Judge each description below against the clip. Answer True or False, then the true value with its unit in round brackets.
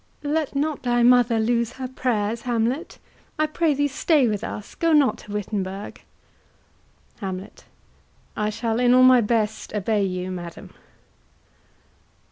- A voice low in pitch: False (235 Hz)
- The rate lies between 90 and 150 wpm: True (135 wpm)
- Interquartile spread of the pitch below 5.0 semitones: True (3.8 semitones)